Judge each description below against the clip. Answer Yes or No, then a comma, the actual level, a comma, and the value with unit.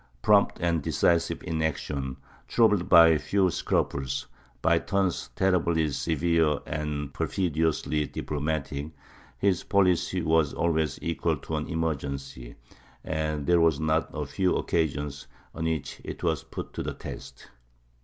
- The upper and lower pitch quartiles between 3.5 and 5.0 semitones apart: No, narrow, 2.5 semitones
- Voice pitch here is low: Yes, very low, 80 Hz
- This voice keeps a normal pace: No, slow, 130 wpm